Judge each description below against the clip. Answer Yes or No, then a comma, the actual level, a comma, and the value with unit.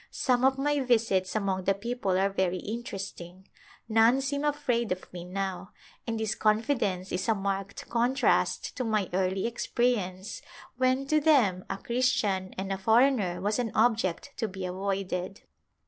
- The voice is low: No, high, 210 Hz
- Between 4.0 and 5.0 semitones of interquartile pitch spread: Yes, average, 4.4 semitones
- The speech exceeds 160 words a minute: No, average, 155 wpm